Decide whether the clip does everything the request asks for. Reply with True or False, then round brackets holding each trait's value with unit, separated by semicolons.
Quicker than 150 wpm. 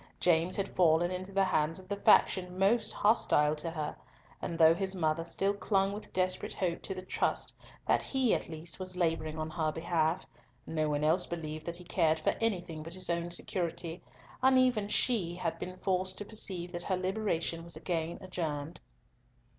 True (185 wpm)